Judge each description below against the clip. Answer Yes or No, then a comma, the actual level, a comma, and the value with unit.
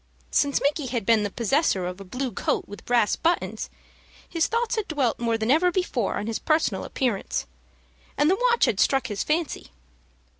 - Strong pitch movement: Yes, wide, 6.7 semitones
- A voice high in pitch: Yes, very high, 260 Hz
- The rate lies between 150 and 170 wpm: No, average, 185 wpm